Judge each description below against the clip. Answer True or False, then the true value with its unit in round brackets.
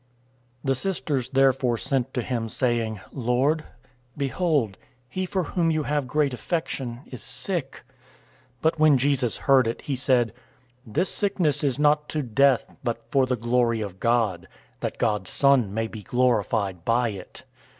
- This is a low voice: True (130 Hz)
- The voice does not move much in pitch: False (3.9 semitones)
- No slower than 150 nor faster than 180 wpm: True (160 wpm)